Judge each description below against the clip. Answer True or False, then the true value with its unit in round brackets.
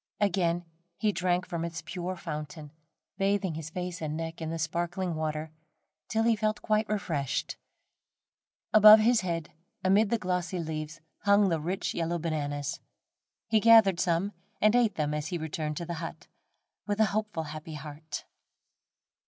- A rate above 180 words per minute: False (155 wpm)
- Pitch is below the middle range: False (170 Hz)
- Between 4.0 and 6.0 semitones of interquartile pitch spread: True (4.3 semitones)